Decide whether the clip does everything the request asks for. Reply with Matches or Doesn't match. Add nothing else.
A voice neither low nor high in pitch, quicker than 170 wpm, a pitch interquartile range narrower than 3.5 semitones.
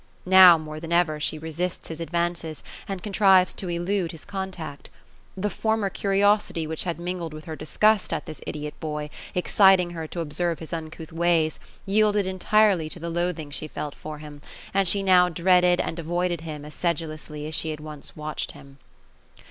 Matches